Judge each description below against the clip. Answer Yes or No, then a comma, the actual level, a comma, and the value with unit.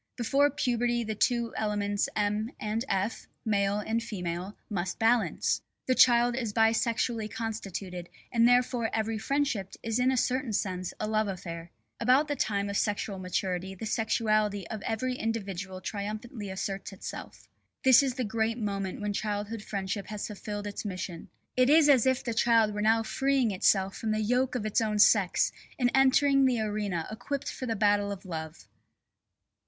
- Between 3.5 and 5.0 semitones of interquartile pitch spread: No, average, 3.0 semitones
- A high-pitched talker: Yes, high, 215 Hz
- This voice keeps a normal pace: Yes, average, 170 wpm